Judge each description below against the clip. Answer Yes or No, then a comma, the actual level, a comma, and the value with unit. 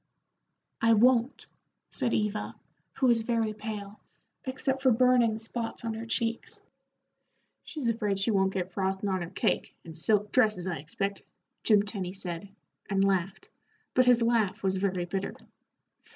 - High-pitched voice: Yes, high, 210 Hz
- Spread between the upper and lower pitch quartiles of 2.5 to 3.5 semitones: Yes, average, 3.2 semitones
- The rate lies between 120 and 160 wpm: Yes, average, 150 wpm